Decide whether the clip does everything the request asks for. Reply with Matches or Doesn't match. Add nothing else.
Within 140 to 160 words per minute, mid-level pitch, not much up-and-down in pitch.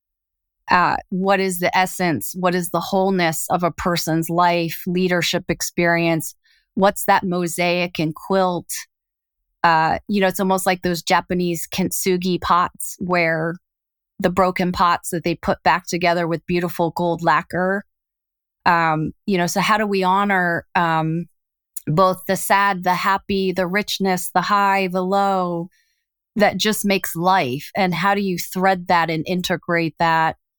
Matches